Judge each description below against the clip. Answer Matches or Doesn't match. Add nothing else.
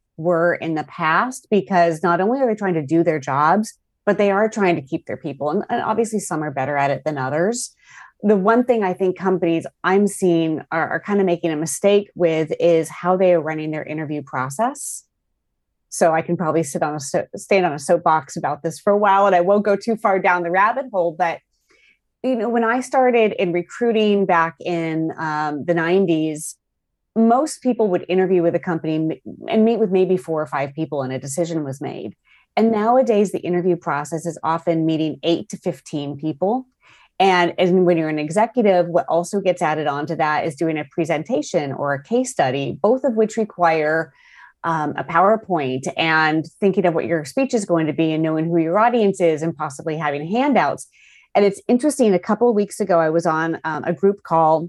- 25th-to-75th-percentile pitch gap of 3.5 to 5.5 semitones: Matches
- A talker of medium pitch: Matches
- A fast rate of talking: Matches